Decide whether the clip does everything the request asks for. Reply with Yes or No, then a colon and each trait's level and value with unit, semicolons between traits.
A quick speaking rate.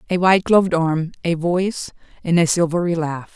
No: average, 180 wpm